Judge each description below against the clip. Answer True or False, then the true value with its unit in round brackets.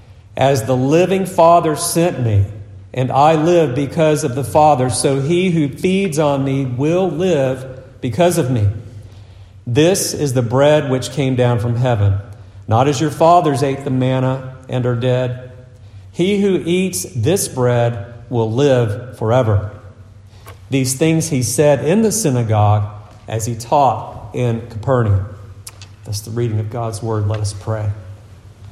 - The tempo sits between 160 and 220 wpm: False (150 wpm)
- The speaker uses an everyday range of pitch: False (5.7 semitones)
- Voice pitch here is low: True (125 Hz)